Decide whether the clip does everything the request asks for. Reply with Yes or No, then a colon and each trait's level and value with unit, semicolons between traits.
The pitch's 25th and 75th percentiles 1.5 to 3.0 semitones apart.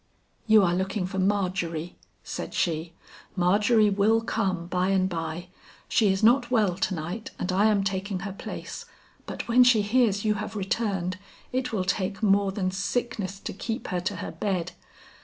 Yes: average, 2.7 semitones